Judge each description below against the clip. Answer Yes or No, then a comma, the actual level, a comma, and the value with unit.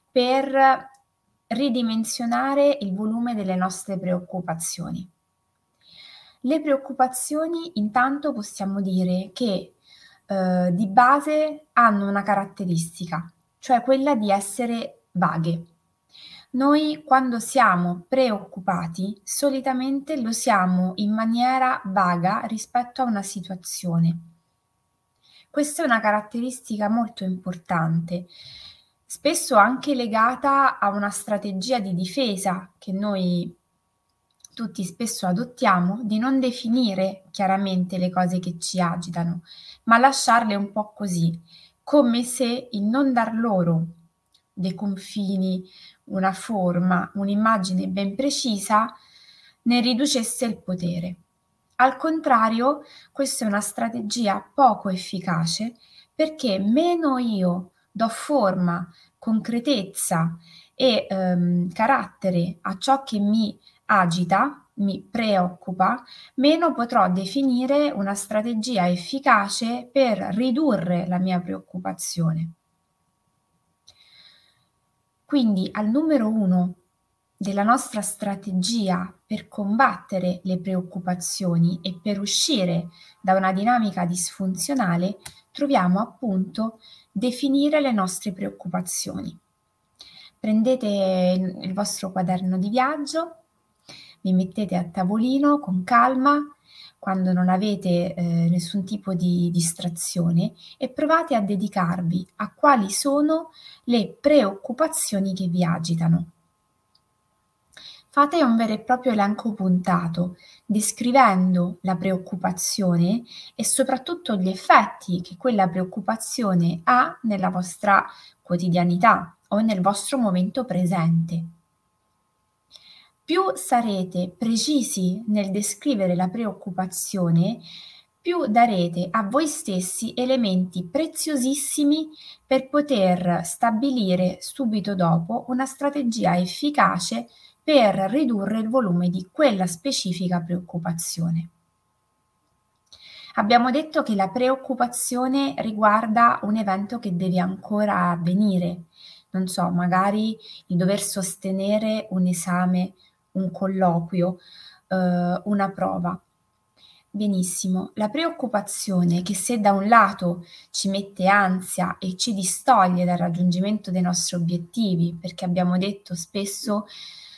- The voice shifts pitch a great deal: No, average, 4.9 semitones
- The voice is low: No, high, 200 Hz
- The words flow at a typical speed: No, slow, 100 wpm